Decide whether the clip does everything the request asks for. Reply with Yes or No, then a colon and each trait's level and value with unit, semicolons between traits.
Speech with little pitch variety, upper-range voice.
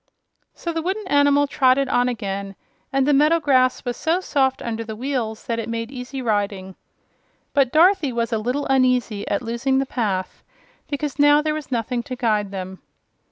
No: average, 4.0 semitones; very high, 255 Hz